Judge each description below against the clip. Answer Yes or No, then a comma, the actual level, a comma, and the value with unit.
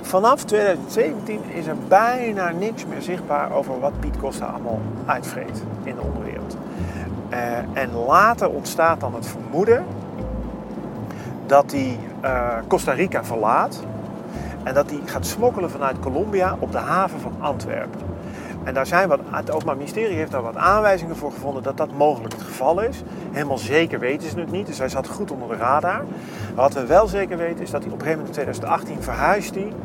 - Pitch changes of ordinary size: No, wide, 7.6 semitones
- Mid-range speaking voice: Yes, medium, 145 Hz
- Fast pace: No, average, 180 wpm